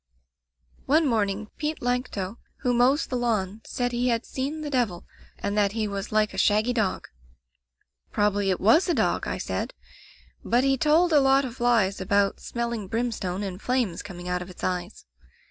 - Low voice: No, high, 220 Hz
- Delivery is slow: No, average, 180 wpm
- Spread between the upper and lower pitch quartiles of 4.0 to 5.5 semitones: Yes, average, 4.3 semitones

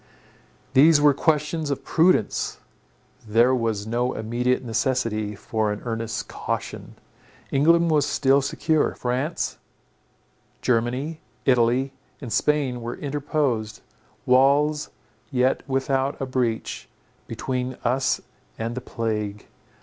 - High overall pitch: No, low, 130 Hz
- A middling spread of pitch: Yes, average, 3.7 semitones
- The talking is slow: Yes, slow, 105 wpm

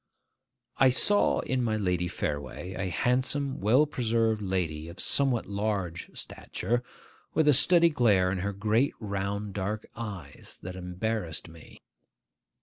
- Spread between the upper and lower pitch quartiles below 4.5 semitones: No, average, 4.9 semitones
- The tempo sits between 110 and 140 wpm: Yes, slow, 135 wpm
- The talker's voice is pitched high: No, low, 105 Hz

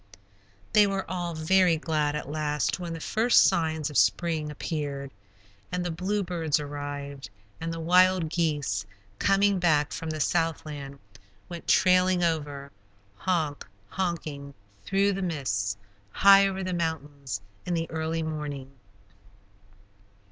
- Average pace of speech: No, slow, 125 wpm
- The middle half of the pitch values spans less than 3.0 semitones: No, average, 3.6 semitones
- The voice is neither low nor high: Yes, medium, 160 Hz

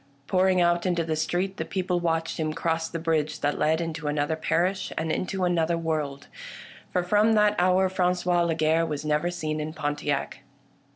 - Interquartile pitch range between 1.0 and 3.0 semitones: Yes, narrow, 2.4 semitones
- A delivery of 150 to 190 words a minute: Yes, average, 180 wpm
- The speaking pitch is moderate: Yes, medium, 165 Hz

